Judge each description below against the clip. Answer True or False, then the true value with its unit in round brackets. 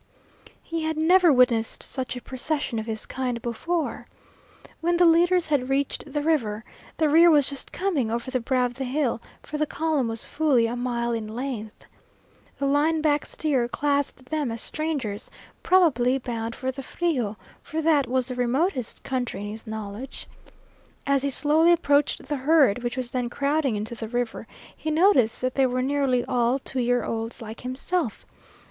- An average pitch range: True (4.2 semitones)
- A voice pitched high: True (260 Hz)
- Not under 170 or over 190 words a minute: True (180 wpm)